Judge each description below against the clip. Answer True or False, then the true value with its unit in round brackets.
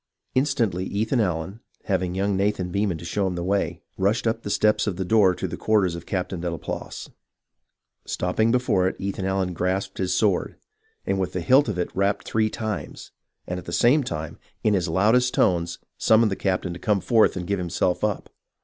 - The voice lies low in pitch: True (95 Hz)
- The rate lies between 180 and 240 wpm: True (195 wpm)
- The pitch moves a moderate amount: True (3.1 semitones)